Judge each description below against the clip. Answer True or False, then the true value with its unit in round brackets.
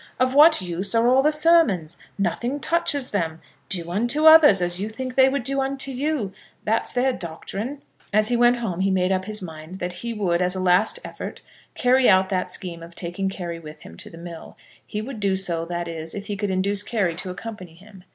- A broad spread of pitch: True (5.9 semitones)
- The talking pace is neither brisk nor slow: False (220 wpm)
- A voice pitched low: False (200 Hz)